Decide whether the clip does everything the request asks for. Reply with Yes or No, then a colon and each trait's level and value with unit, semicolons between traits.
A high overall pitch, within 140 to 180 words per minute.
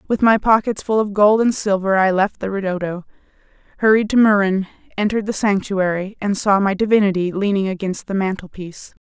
Yes: high, 200 Hz; average, 175 wpm